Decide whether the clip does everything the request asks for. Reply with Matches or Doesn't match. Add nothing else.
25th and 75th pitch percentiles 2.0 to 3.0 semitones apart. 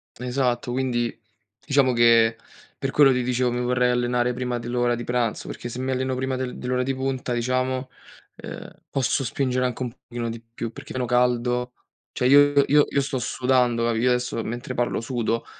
Doesn't match